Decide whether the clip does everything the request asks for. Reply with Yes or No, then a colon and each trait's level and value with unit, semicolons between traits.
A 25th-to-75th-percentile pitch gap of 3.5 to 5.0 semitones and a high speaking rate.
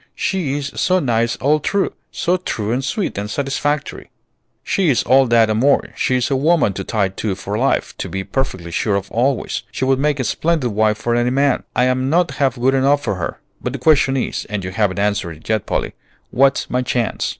Yes: average, 4.5 semitones; fast, 210 wpm